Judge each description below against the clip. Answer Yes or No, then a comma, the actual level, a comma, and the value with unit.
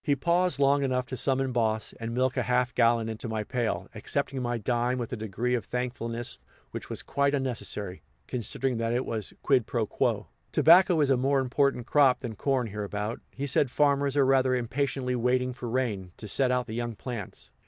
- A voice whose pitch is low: Yes, low, 125 Hz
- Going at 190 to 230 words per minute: Yes, average, 195 wpm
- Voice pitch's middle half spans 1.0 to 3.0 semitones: Yes, average, 2.7 semitones